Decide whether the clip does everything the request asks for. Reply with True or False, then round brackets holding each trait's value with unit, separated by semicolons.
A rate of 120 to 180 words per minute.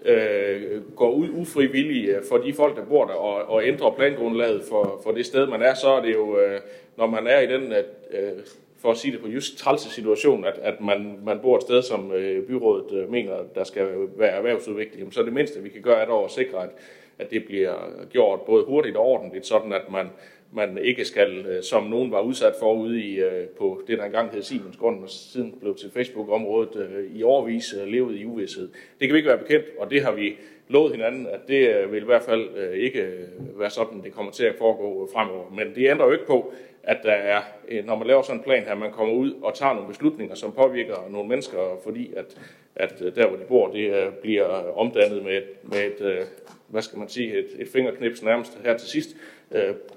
False (215 wpm)